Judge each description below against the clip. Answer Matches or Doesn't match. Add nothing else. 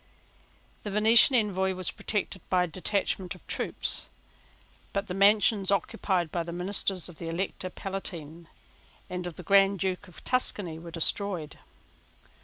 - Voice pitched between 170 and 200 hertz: Matches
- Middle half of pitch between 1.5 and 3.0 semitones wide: Matches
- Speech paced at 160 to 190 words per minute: Doesn't match